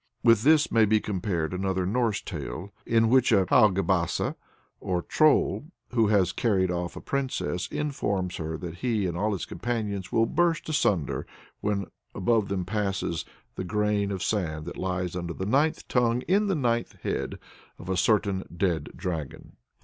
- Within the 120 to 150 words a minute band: No, average, 165 wpm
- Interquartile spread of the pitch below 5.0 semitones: Yes, average, 4.3 semitones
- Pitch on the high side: No, low, 100 Hz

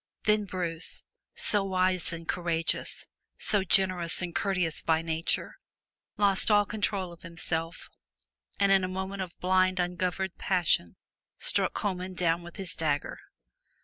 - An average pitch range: No, narrow, 2.3 semitones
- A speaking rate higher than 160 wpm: No, slow, 135 wpm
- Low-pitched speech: No, medium, 185 Hz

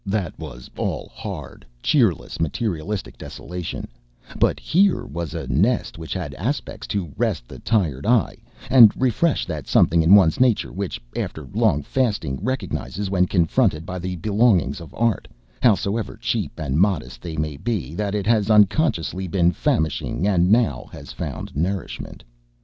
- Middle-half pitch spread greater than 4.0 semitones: Yes, wide, 5.4 semitones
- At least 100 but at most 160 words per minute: Yes, average, 150 wpm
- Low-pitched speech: Yes, very low, 95 Hz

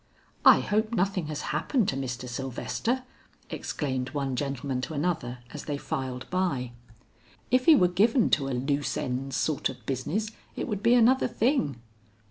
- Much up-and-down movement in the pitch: Yes, wide, 8.2 semitones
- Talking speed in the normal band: Yes, average, 160 wpm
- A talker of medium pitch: Yes, medium, 145 Hz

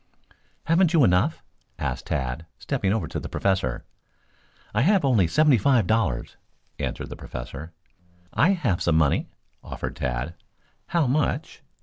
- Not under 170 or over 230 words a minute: No, slow, 135 wpm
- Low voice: Yes, low, 100 Hz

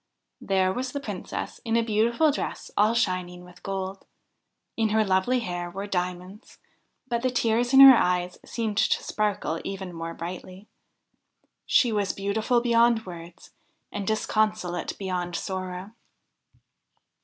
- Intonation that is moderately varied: Yes, average, 4.1 semitones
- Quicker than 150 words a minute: No, slow, 135 wpm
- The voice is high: Yes, high, 200 Hz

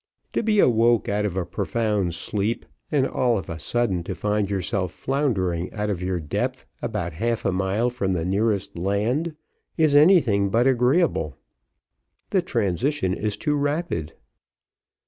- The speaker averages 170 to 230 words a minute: No, average, 150 wpm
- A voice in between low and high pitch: No, low, 105 Hz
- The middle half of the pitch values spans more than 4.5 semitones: Yes, average, 4.9 semitones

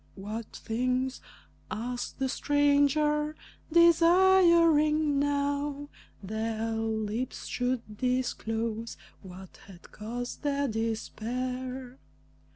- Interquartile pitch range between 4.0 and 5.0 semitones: Yes, average, 4.4 semitones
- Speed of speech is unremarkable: No, slow, 75 wpm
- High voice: Yes, very high, 255 Hz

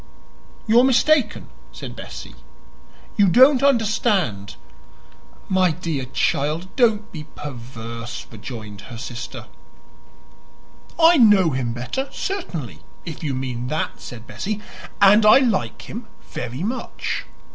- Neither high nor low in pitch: Yes, medium, 170 Hz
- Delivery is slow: Yes, slow, 115 wpm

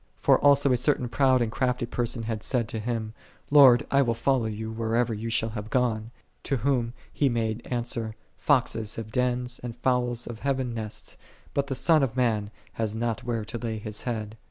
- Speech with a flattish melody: Yes, narrow, 2.2 semitones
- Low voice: Yes, low, 120 Hz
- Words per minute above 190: Yes, average, 200 wpm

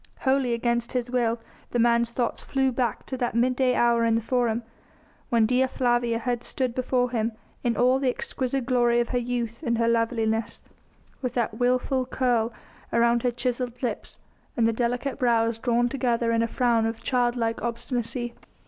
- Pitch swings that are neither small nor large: No, narrow, 1.3 semitones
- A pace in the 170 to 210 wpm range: Yes, average, 175 wpm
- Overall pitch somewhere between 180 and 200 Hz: No, high, 240 Hz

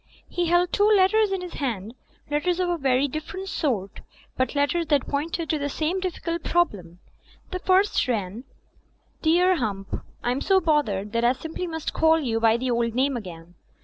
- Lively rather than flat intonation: Yes, wide, 6.9 semitones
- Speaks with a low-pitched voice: No, very high, 295 Hz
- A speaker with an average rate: Yes, average, 180 wpm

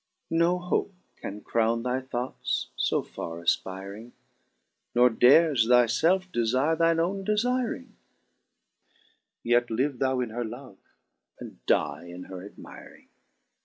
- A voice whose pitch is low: Yes, low, 125 Hz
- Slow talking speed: Yes, slow, 125 wpm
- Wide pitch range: Yes, wide, 6.7 semitones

